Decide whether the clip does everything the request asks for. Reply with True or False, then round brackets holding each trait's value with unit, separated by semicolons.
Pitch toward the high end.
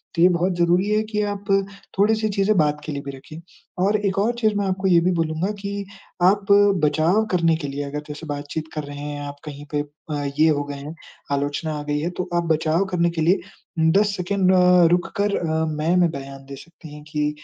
False (170 Hz)